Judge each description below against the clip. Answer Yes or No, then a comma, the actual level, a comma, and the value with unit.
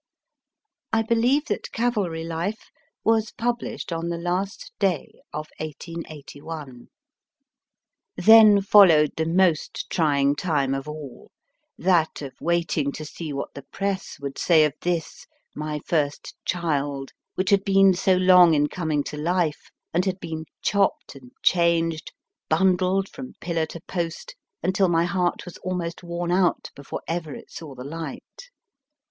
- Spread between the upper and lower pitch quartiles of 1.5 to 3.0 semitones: No, average, 3.5 semitones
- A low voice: No, medium, 170 Hz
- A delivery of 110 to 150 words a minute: Yes, average, 140 wpm